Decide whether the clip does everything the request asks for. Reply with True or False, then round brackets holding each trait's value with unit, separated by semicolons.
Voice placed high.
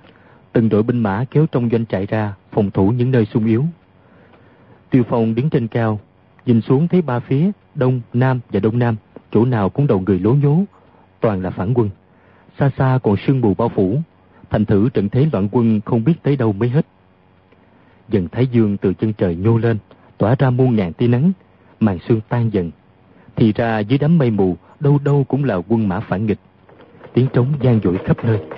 False (115 Hz)